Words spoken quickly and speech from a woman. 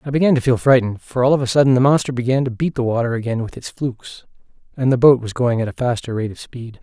No: fast, 280 wpm; male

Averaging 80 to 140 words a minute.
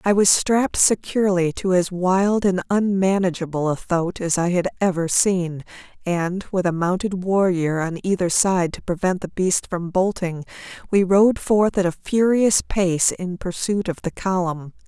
No: average, 170 wpm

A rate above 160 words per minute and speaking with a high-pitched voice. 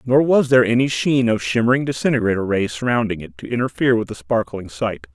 No: average, 200 wpm; low, 115 Hz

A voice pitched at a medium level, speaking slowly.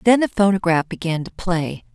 No: medium, 180 Hz; average, 185 wpm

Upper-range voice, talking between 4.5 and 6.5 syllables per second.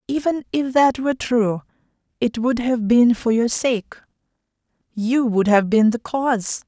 No: high, 240 Hz; 4.3 syllables/s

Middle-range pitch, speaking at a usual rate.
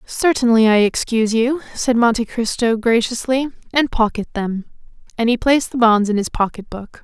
No: high, 230 Hz; average, 170 wpm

